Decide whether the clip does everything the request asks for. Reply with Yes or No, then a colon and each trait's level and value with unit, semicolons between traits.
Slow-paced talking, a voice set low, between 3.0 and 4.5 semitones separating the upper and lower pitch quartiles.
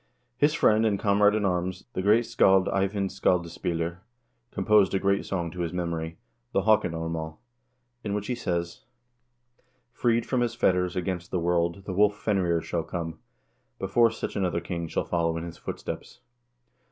No: average, 165 wpm; very low, 95 Hz; average, 3.3 semitones